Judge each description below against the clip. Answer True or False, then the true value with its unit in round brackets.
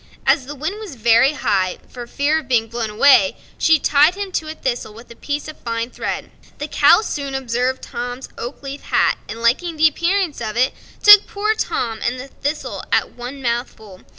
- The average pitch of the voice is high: True (265 Hz)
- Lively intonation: False (4.7 semitones)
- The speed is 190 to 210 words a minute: True (200 wpm)